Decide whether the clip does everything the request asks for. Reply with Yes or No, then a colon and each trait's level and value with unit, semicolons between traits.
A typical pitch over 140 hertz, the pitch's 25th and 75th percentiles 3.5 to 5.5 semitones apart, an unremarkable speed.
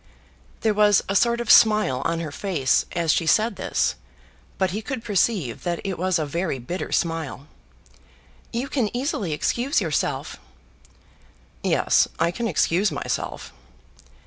Yes: high, 190 Hz; average, 5.1 semitones; average, 145 wpm